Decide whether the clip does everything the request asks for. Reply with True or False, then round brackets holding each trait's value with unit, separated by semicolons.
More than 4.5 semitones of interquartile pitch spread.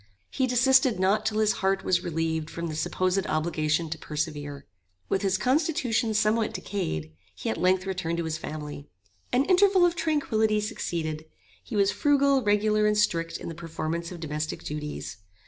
True (5.6 semitones)